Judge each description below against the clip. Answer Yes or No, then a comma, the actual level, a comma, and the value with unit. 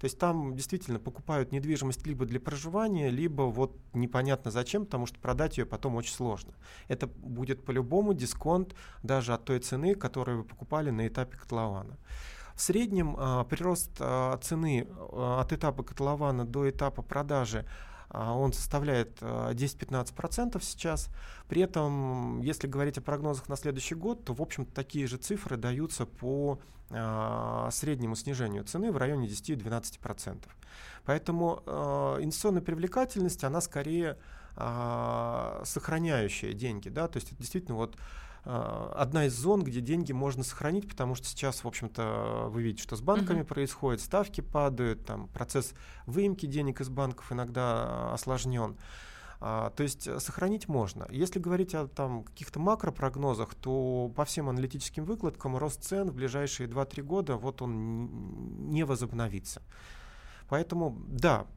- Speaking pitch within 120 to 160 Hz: Yes, low, 135 Hz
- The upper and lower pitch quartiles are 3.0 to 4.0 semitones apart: No, average, 4.4 semitones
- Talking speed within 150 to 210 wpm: No, average, 135 wpm